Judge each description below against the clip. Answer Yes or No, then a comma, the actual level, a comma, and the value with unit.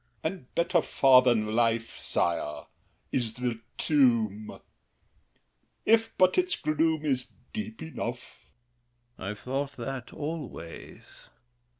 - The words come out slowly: Yes, slow, 115 wpm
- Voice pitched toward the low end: Yes, low, 130 Hz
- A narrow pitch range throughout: No, wide, 5.6 semitones